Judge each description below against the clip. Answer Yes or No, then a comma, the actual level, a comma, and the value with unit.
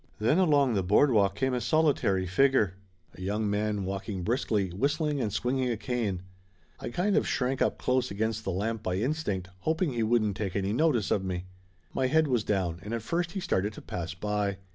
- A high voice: No, low, 110 Hz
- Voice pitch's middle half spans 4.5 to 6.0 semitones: Yes, average, 5.2 semitones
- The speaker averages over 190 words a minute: Yes, average, 200 wpm